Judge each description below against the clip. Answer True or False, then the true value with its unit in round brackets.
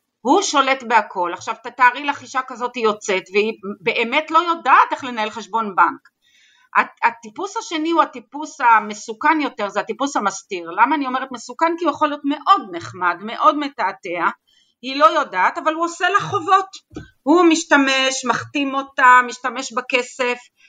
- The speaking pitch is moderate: False (265 Hz)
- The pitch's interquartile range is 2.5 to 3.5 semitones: False (5.2 semitones)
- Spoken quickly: True (155 wpm)